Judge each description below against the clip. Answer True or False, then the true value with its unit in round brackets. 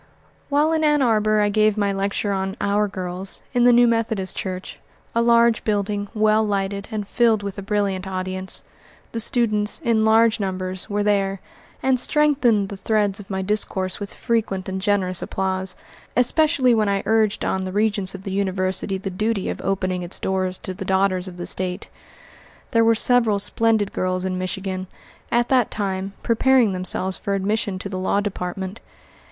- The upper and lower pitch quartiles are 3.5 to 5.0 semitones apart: False (2.7 semitones)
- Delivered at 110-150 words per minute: False (175 wpm)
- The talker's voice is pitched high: True (200 Hz)